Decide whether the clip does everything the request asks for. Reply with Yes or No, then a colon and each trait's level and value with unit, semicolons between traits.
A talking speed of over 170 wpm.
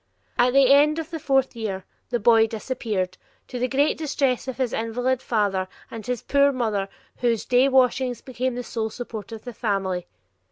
Yes: average, 185 wpm